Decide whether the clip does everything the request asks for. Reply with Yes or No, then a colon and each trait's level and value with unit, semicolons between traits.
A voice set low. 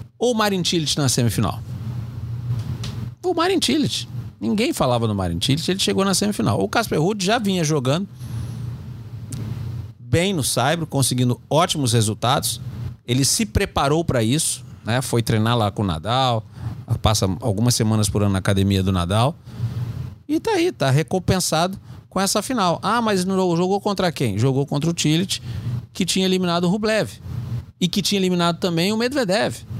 Yes: low, 125 Hz